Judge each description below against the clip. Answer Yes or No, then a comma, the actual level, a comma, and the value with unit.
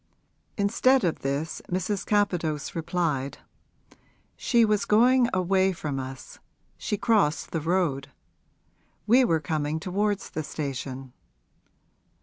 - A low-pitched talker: No, medium, 175 Hz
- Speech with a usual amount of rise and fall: No, wide, 5.8 semitones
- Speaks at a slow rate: Yes, slow, 110 wpm